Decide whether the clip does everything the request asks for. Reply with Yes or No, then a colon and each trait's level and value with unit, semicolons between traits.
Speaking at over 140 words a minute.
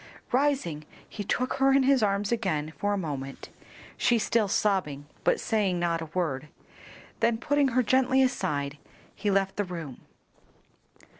Yes: average, 150 wpm